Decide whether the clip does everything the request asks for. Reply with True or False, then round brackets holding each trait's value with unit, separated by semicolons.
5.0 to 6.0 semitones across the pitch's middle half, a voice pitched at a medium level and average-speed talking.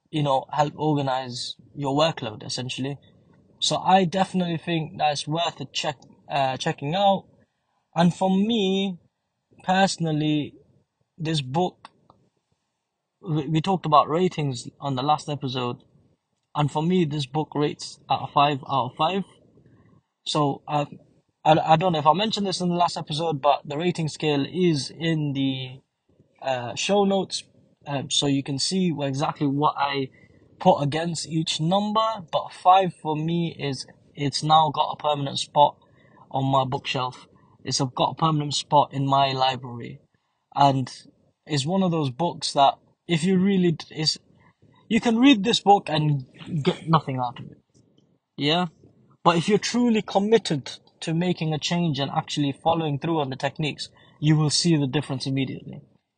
False (3.6 semitones; 150 Hz; 155 wpm)